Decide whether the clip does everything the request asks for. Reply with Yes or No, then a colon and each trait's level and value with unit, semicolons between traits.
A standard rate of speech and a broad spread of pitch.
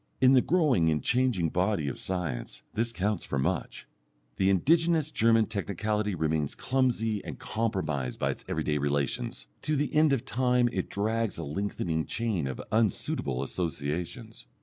Yes: average, 150 wpm; wide, 7.1 semitones